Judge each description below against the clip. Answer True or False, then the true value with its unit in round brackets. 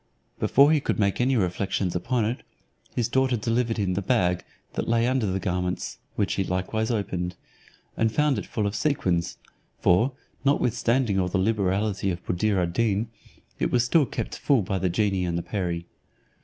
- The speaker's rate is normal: True (175 wpm)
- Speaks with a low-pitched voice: True (105 Hz)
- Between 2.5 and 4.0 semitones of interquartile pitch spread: False (4.5 semitones)